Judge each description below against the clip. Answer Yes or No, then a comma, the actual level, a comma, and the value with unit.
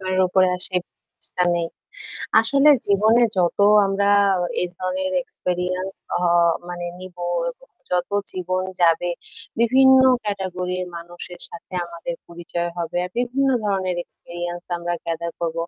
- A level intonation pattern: Yes, narrow, 2.0 semitones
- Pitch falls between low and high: Yes, medium, 180 Hz